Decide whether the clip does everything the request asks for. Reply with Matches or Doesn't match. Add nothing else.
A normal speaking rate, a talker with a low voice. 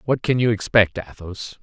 Matches